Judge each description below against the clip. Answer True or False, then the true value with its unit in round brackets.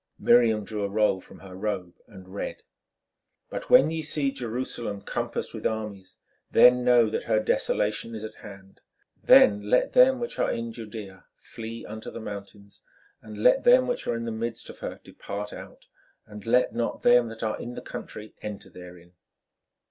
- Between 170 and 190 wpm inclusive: True (180 wpm)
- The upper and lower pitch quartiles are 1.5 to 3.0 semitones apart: True (2.7 semitones)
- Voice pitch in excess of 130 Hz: False (110 Hz)